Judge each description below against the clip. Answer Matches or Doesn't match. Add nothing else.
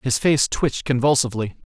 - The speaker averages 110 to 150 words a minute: Matches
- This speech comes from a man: Matches